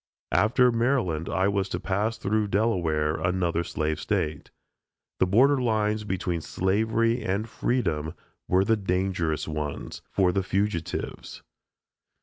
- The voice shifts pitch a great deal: No, average, 4.3 semitones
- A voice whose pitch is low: Yes, very low, 95 Hz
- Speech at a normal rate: No, slow, 125 wpm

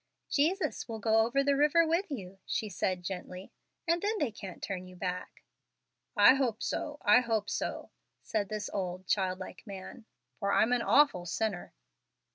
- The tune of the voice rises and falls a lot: Yes, wide, 6.6 semitones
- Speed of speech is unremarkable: Yes, average, 170 wpm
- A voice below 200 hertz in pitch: No, high, 215 Hz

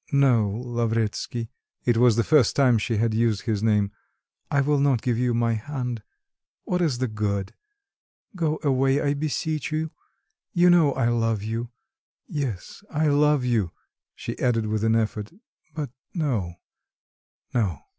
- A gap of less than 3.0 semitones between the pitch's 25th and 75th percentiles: No, average, 4.4 semitones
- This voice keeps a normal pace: Yes, average, 150 wpm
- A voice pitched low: Yes, low, 120 Hz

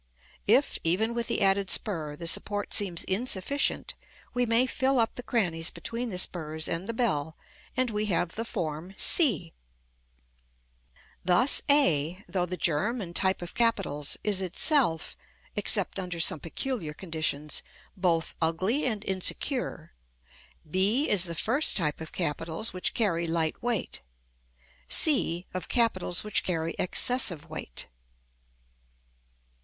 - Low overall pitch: No, medium, 185 Hz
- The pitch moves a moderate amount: No, wide, 5.7 semitones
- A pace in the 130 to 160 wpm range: Yes, slow, 135 wpm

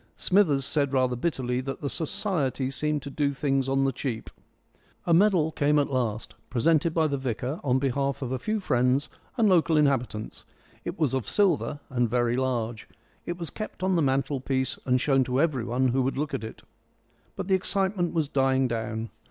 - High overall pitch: No, low, 135 Hz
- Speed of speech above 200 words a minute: No, average, 185 wpm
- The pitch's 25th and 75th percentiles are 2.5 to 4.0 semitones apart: Yes, average, 3.7 semitones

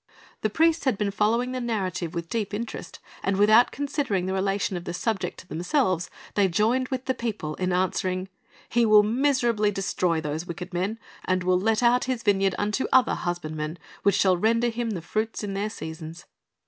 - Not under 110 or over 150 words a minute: No, average, 185 wpm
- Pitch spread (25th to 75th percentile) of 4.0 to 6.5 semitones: Yes, average, 4.3 semitones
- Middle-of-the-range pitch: No, high, 205 Hz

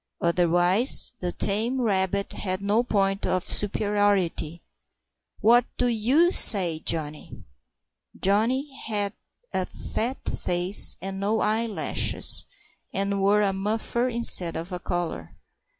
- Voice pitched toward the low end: No, high, 200 Hz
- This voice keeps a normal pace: No, slow, 115 wpm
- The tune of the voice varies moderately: Yes, average, 3.5 semitones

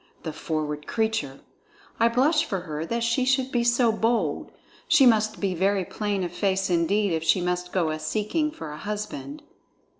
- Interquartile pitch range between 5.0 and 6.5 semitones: Yes, wide, 5.6 semitones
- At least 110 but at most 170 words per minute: No, average, 180 wpm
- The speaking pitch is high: Yes, high, 205 Hz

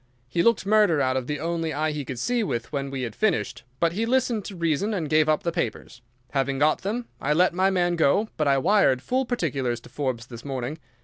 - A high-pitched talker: No, medium, 155 Hz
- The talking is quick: Yes, fast, 235 wpm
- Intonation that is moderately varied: No, wide, 6.2 semitones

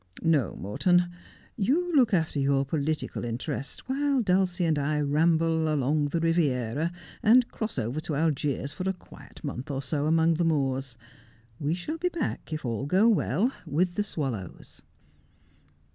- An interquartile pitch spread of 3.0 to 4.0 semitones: No, average, 4.6 semitones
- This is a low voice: No, medium, 160 Hz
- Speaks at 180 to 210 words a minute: No, average, 155 wpm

